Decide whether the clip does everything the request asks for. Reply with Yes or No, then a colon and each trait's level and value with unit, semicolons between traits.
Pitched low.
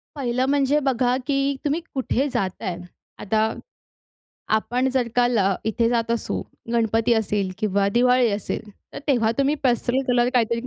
No: high, 240 Hz